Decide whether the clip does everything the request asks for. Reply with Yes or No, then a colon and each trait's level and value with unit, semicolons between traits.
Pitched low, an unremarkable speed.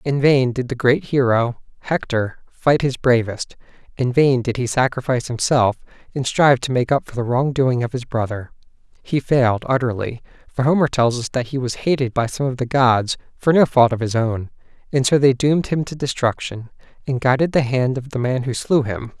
No: low, 130 Hz; fast, 210 wpm